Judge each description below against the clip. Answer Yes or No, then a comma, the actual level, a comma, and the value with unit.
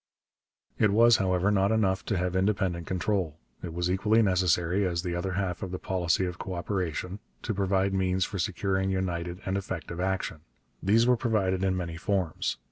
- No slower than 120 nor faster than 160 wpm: No, average, 180 wpm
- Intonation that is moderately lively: No, narrow, 1.8 semitones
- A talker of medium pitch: No, very low, 95 Hz